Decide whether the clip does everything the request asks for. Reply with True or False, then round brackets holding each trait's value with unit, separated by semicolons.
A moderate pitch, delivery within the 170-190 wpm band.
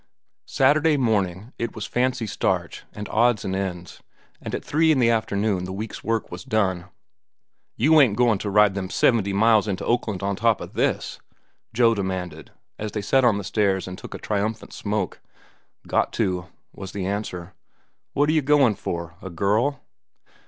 False (105 Hz; 175 wpm)